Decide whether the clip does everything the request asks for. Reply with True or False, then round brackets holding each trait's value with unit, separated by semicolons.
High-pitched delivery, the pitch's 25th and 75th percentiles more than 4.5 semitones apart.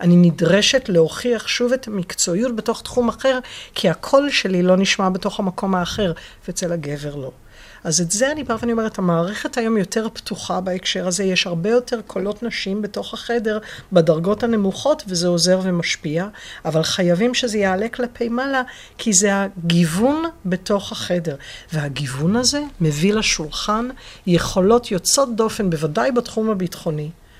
True (195 Hz; 5.1 semitones)